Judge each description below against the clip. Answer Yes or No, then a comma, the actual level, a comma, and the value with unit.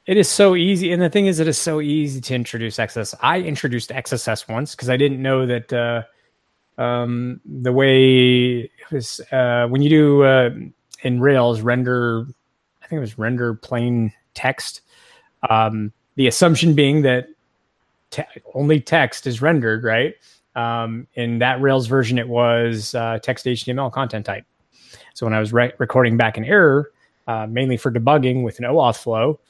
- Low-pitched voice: Yes, low, 125 Hz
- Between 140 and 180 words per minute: Yes, average, 175 wpm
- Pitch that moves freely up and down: No, average, 3.1 semitones